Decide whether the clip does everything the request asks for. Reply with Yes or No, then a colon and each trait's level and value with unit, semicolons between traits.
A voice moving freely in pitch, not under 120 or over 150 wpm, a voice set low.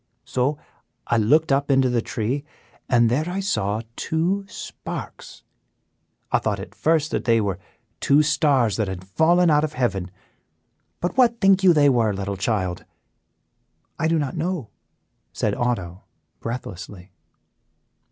Yes: wide, 7.0 semitones; average, 140 wpm; low, 130 Hz